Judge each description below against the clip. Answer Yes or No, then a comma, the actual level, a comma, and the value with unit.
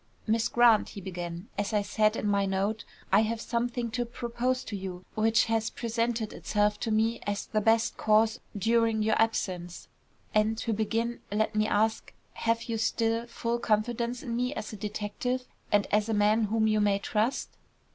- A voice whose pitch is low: No, high, 220 Hz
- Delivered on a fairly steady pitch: Yes, narrow, 1.8 semitones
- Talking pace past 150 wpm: Yes, average, 180 wpm